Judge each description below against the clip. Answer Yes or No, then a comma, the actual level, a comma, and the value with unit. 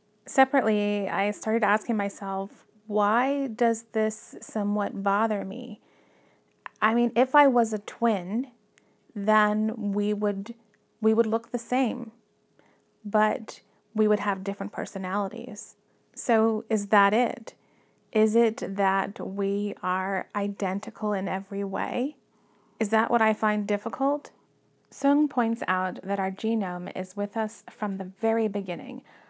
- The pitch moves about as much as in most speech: No, narrow, 2.3 semitones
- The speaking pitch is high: Yes, high, 215 Hz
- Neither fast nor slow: No, slow, 130 wpm